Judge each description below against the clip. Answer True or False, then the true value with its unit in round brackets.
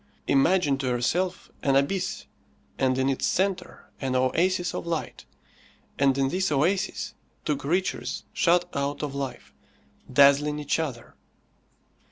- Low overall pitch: False (145 Hz)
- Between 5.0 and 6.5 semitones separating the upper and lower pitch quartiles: False (4.6 semitones)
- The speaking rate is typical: False (130 wpm)